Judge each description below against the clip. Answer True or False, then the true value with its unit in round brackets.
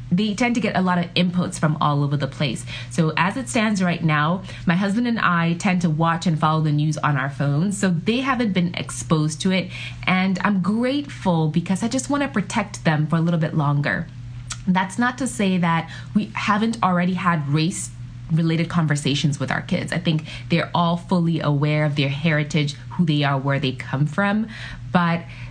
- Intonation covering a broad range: False (4.0 semitones)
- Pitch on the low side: False (165 Hz)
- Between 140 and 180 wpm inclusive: False (205 wpm)